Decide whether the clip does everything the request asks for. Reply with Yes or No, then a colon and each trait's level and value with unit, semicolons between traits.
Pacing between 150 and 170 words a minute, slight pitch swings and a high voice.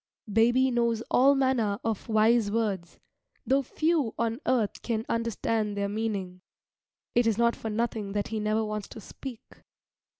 Yes: average, 155 wpm; narrow, 2.1 semitones; high, 225 Hz